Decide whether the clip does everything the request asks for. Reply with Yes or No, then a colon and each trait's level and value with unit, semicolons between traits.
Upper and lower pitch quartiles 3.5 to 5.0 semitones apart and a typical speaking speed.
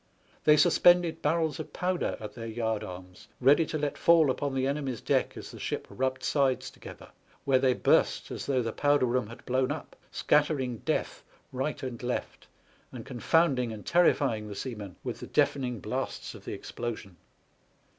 Yes: average, 4.0 semitones; average, 180 wpm